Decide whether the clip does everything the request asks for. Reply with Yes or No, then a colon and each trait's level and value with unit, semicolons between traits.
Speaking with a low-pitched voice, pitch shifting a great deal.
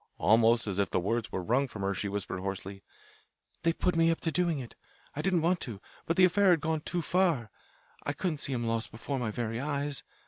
Yes: low, 130 Hz; wide, 7.2 semitones